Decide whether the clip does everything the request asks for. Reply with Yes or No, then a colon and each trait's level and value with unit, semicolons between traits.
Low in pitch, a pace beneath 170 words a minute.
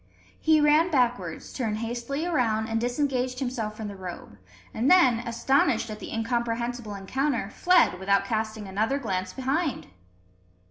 No: high, 235 Hz; average, 140 wpm